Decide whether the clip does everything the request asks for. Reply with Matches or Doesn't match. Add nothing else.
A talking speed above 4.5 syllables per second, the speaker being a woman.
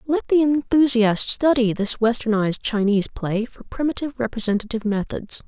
Matches